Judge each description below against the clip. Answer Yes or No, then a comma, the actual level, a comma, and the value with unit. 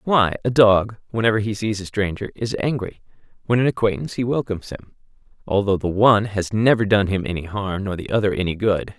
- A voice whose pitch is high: No, low, 105 Hz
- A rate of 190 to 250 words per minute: Yes, average, 200 wpm